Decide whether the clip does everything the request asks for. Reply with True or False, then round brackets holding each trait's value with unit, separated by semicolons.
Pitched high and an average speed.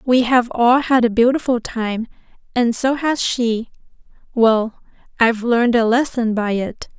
True (235 Hz; 145 wpm)